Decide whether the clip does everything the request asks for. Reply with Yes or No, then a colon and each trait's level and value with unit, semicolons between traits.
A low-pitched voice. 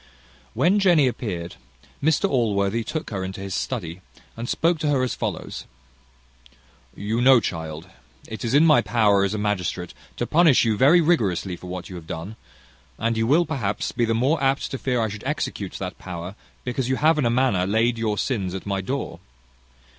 Yes: low, 115 Hz